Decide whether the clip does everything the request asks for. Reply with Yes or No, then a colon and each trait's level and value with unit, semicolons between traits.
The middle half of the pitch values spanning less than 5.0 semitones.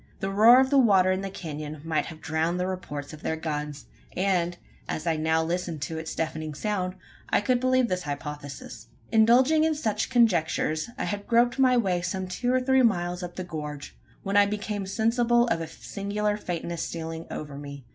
No: wide, 5.5 semitones